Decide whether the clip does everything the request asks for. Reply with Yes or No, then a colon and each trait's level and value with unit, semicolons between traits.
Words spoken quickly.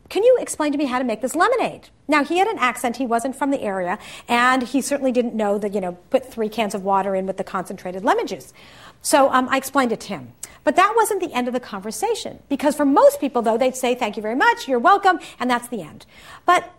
Yes: fast, 255 wpm